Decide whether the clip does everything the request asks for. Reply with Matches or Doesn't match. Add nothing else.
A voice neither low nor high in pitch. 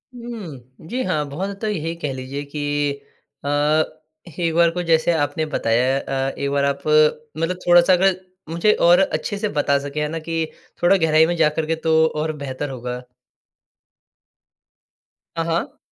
Matches